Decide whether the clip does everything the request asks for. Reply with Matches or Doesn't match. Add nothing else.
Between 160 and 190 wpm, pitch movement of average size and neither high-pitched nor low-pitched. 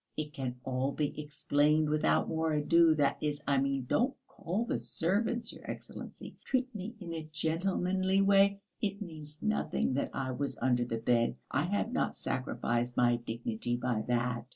Doesn't match